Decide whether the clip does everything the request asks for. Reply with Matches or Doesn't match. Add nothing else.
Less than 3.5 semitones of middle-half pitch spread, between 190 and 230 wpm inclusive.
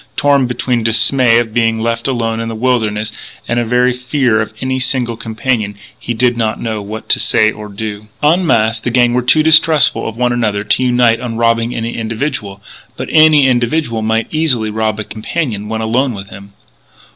Matches